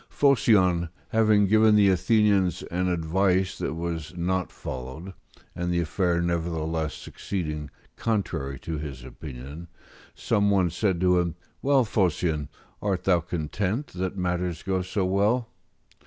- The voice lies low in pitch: Yes, very low, 90 Hz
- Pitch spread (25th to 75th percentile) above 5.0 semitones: No, average, 3.3 semitones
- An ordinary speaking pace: No, slow, 130 wpm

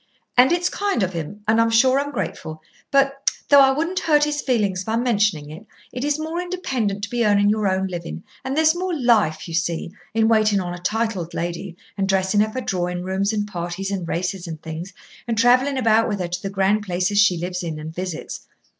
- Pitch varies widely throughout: Yes, wide, 5.9 semitones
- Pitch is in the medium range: No, high, 205 Hz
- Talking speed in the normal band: No, fast, 215 wpm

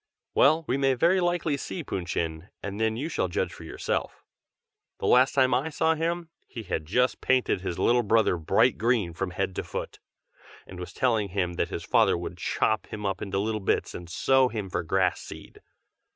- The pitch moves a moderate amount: No, wide, 6.2 semitones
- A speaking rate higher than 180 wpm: Yes, average, 200 wpm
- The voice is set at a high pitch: No, low, 110 Hz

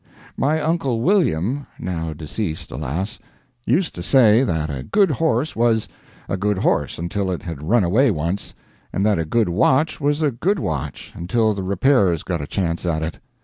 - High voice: No, low, 100 Hz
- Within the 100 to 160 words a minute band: No, average, 180 wpm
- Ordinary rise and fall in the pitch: No, wide, 8.1 semitones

